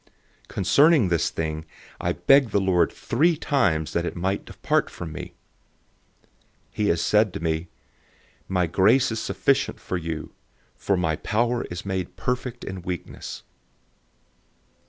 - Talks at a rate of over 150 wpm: No, average, 145 wpm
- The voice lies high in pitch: No, very low, 95 Hz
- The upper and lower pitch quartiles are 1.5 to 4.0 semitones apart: No, wide, 5.6 semitones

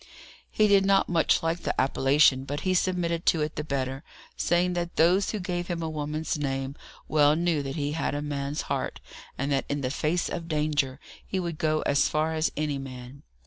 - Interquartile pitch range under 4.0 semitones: Yes, average, 3.4 semitones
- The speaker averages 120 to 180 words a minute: No, fast, 205 wpm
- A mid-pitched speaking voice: Yes, medium, 155 Hz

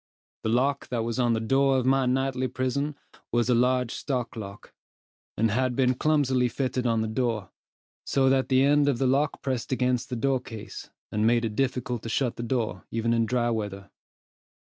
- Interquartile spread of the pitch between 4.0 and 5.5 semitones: No, narrow, 2.5 semitones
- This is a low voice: Yes, low, 125 Hz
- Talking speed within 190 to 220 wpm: Yes, average, 195 wpm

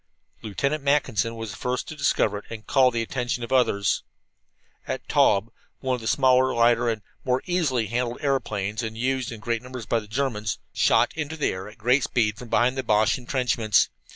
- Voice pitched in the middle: No, low, 120 Hz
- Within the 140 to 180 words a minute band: No, average, 200 wpm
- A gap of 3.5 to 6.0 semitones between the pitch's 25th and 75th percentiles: No, average, 3.1 semitones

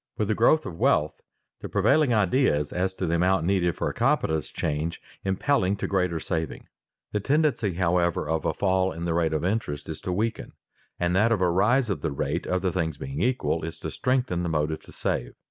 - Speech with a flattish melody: No, average, 4.2 semitones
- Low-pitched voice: Yes, very low, 90 Hz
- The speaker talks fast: Yes, fast, 210 wpm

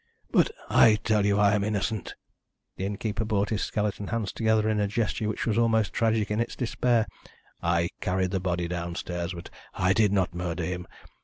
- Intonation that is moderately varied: Yes, average, 3.2 semitones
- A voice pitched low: Yes, low, 105 Hz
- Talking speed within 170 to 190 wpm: Yes, average, 185 wpm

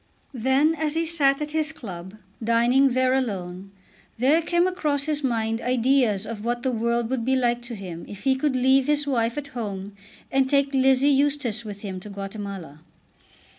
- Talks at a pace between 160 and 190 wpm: Yes, average, 180 wpm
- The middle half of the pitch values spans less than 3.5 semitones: No, average, 4.3 semitones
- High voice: Yes, very high, 255 Hz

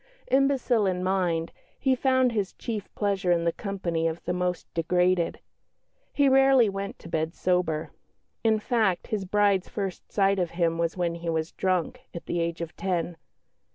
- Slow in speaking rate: No, average, 170 wpm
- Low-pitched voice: No, medium, 185 Hz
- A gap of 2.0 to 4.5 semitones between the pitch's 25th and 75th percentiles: Yes, average, 3.8 semitones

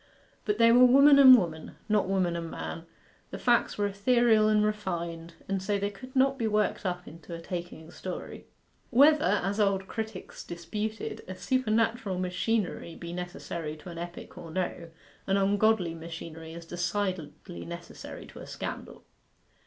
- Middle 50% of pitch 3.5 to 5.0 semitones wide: Yes, average, 4.2 semitones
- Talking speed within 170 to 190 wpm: No, average, 160 wpm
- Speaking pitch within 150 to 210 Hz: Yes, high, 190 Hz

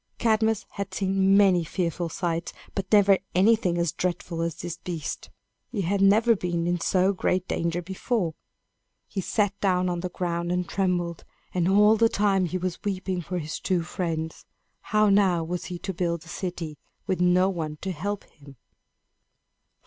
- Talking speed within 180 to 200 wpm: No, average, 170 wpm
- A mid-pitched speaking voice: Yes, medium, 180 Hz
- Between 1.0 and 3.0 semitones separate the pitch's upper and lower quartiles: Yes, narrow, 2.4 semitones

